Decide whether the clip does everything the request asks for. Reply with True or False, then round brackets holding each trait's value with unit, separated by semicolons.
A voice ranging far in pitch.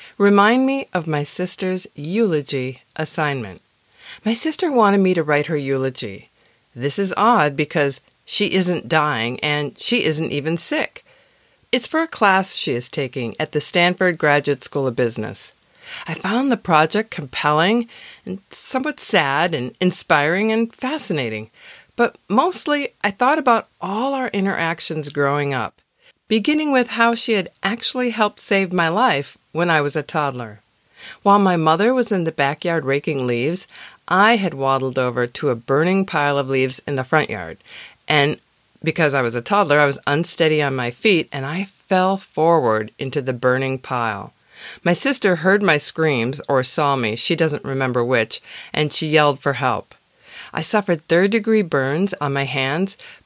True (6.6 semitones)